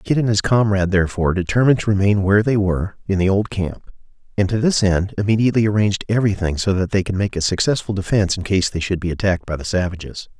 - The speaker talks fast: Yes, fast, 225 wpm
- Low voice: Yes, low, 100 Hz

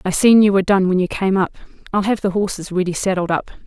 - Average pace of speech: No, fast, 260 wpm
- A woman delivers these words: Yes, female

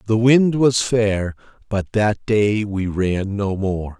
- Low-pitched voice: Yes, low, 105 Hz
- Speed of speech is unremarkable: Yes, average, 165 wpm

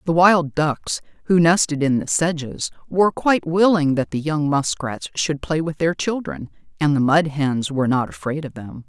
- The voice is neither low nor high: Yes, medium, 150 Hz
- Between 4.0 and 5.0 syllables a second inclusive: Yes, 4.8 syllables/s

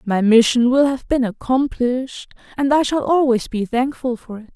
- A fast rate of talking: No, average, 185 wpm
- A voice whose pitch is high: Yes, very high, 250 Hz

